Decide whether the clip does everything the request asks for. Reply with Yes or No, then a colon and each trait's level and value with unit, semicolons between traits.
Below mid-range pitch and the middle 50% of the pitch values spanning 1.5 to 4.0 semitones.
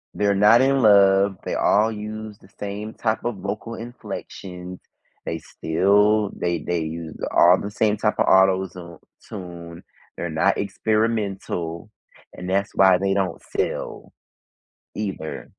Yes: low, 100 Hz; average, 2.9 semitones